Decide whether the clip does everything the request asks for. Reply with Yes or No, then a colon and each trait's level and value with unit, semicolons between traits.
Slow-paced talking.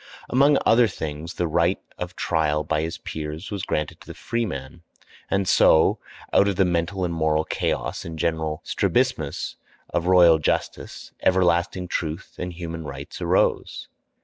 No: average, 150 wpm